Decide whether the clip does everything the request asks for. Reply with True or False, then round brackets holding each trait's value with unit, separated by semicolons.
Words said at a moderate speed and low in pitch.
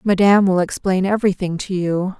False (165 wpm; 190 Hz)